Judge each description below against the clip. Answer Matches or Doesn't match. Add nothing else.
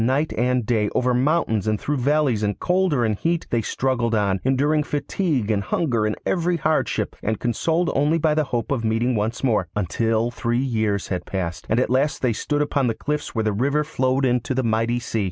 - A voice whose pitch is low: Matches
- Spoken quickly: Matches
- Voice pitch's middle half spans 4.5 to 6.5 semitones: Matches